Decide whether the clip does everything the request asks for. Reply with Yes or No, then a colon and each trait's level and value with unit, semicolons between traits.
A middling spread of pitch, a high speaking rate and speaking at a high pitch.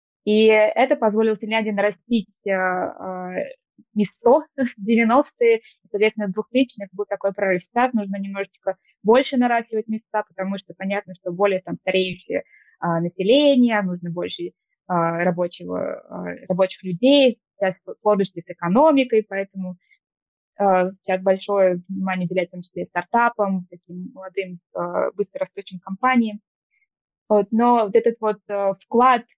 No: average, 3.8 semitones; average, 130 wpm; high, 200 Hz